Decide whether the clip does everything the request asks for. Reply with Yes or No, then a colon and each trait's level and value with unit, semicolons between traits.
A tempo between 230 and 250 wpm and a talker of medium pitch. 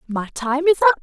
No: fast, 235 wpm; very high, 290 Hz